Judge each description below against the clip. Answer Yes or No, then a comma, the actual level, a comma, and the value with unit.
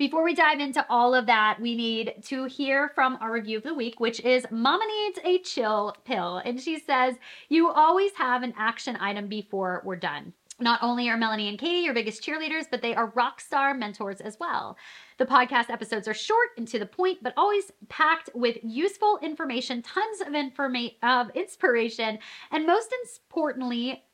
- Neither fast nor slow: Yes, average, 190 wpm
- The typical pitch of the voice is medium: No, very high, 250 Hz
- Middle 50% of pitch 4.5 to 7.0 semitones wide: Yes, wide, 5.5 semitones